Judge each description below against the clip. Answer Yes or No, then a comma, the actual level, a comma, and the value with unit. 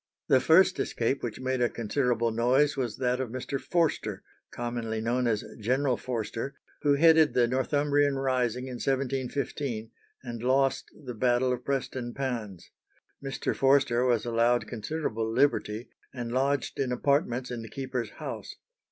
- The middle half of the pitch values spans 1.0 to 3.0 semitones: Yes, narrow, 2.5 semitones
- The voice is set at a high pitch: No, low, 125 Hz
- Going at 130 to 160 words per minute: Yes, average, 145 wpm